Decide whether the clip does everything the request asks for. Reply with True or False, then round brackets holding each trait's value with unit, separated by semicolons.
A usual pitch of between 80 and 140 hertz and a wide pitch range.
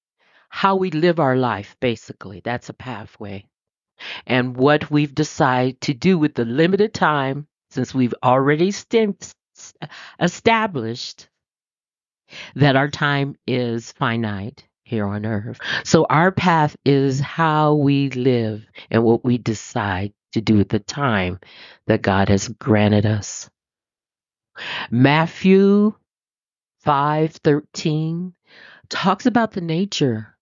True (135 Hz; 5.7 semitones)